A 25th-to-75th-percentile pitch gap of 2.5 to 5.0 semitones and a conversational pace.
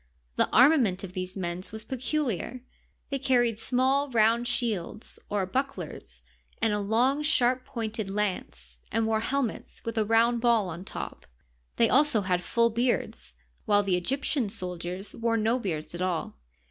Yes: average, 4.7 semitones; average, 155 wpm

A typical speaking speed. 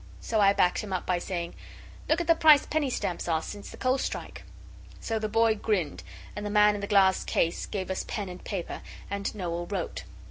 No: fast, 215 wpm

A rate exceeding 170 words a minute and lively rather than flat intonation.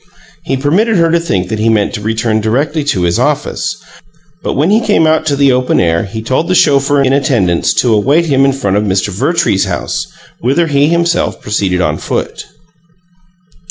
Yes: average, 195 wpm; wide, 6.8 semitones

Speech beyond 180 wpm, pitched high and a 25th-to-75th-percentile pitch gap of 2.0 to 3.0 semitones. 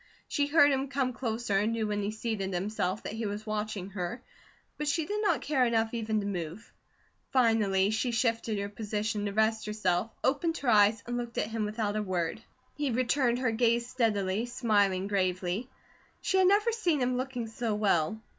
No: average, 190 wpm; high, 220 Hz; average, 3.4 semitones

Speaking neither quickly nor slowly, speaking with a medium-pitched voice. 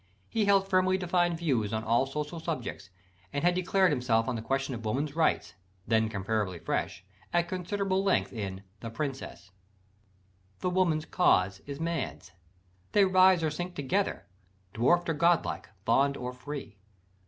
Yes: average, 155 wpm; medium, 150 Hz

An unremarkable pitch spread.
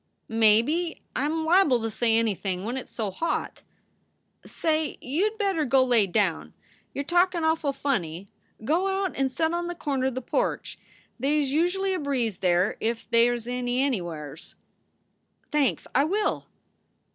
No: wide, 6.4 semitones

